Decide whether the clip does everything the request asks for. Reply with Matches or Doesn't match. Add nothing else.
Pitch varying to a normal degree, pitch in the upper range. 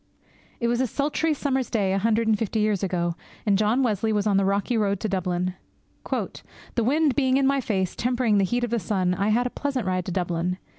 Matches